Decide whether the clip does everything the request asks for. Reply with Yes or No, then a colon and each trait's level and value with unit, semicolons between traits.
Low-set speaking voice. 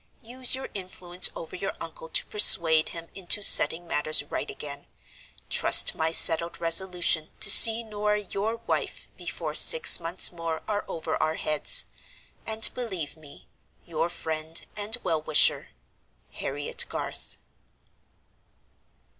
No: medium, 175 Hz